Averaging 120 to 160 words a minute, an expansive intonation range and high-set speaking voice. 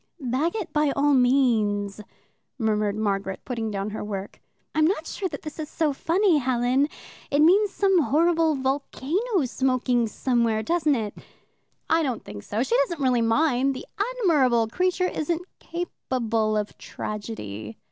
Yes: average, 145 wpm; wide, 6.4 semitones; very high, 265 Hz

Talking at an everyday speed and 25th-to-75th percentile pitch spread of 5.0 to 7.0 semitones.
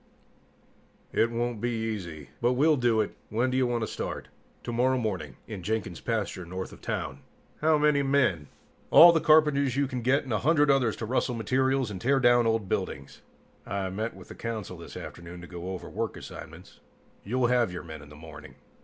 Yes: average, 195 wpm; wide, 5.5 semitones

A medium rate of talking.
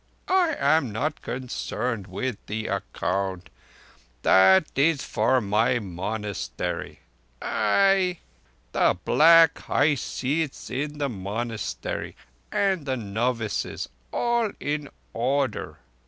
No: slow, 95 wpm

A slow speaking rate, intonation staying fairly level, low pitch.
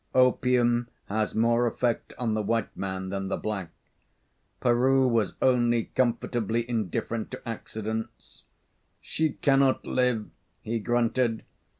Yes: slow, 115 wpm; narrow, 2.3 semitones; low, 115 Hz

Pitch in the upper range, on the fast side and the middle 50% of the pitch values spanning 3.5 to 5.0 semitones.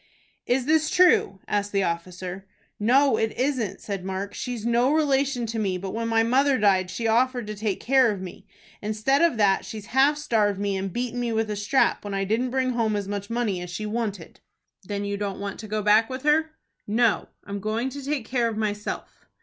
Yes: high, 220 Hz; fast, 215 wpm; average, 3.8 semitones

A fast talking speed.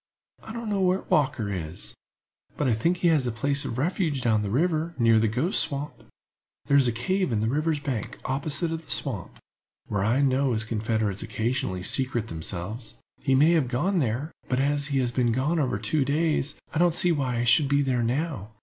Yes: fast, 210 wpm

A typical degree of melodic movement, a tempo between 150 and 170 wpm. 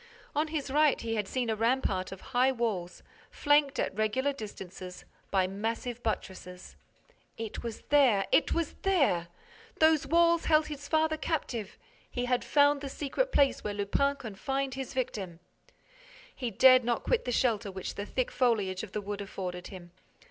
No: wide, 5.8 semitones; average, 165 wpm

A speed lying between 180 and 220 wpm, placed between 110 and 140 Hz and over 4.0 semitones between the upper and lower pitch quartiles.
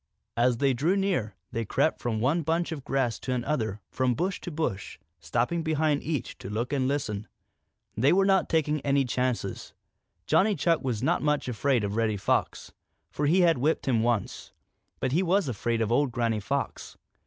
Yes: average, 190 wpm; low, 135 Hz; average, 5.2 semitones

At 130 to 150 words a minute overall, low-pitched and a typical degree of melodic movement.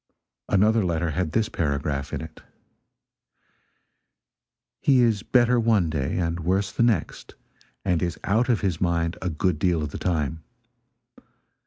Yes: average, 145 wpm; very low, 90 Hz; average, 4.9 semitones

